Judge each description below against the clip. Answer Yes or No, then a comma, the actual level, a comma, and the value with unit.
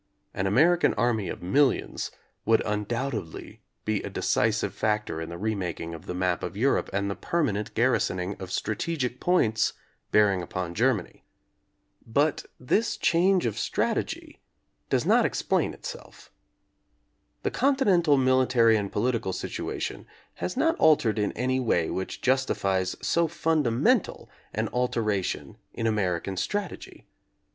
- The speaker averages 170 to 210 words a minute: No, average, 140 wpm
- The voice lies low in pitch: Yes, low, 115 Hz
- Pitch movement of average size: No, wide, 6.0 semitones